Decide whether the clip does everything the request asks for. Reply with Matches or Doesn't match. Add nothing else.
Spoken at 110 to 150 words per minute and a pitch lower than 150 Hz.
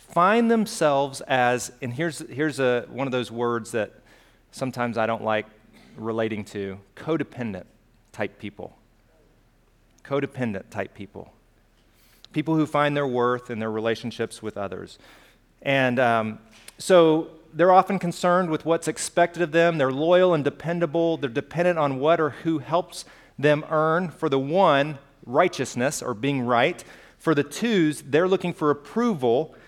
Matches